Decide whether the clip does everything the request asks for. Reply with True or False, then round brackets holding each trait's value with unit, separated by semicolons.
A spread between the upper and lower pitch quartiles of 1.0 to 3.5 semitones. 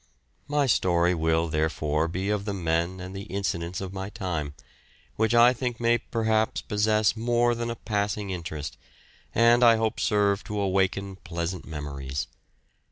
False (4.7 semitones)